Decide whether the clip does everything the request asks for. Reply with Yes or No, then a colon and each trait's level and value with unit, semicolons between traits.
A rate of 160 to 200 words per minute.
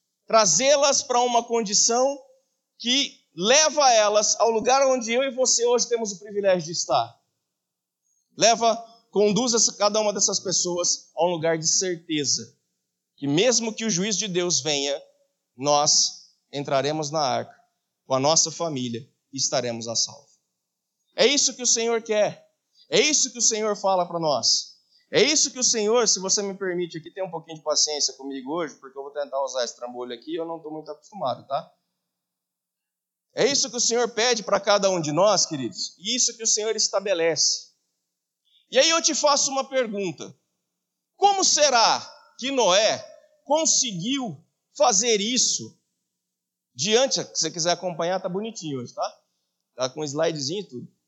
Yes: average, 165 wpm